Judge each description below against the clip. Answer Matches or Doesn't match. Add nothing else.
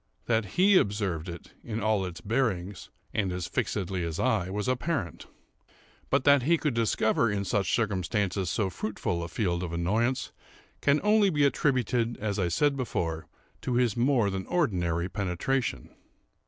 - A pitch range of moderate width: Doesn't match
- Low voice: Matches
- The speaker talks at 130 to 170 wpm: Matches